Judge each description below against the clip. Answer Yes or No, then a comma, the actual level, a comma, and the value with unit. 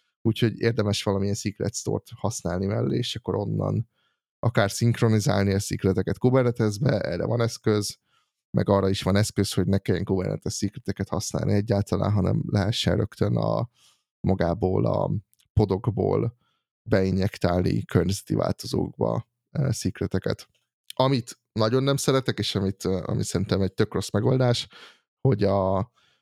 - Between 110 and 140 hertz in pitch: No, low, 100 Hz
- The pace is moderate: Yes, average, 125 wpm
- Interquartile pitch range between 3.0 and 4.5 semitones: Yes, average, 3.4 semitones